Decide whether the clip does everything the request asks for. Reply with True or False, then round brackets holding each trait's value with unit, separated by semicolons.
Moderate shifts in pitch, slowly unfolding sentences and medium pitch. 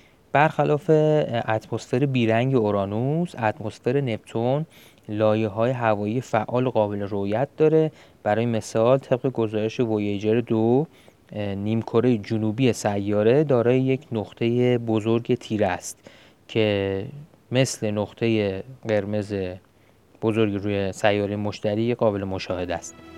False (3.1 semitones; 100 wpm; 110 Hz)